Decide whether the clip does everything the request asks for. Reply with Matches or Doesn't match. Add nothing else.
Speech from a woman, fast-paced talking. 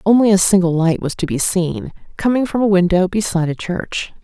Matches